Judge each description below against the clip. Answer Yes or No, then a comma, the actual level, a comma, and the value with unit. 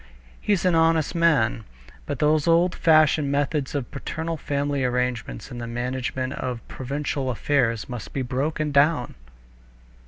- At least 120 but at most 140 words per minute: Yes, slow, 135 wpm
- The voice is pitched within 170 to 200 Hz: No, medium, 140 Hz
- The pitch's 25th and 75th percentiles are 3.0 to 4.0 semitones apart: Yes, average, 3.7 semitones